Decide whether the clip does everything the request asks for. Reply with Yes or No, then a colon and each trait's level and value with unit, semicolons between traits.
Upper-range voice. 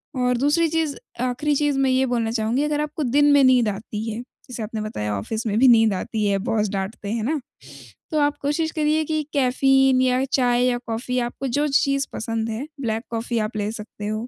Yes: very high, 250 Hz